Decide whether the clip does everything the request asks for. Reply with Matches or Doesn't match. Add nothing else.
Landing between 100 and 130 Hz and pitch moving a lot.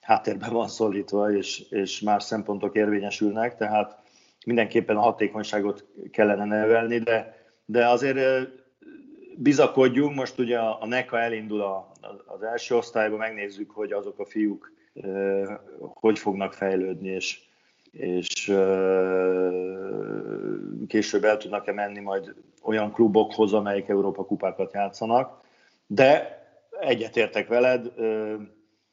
Doesn't match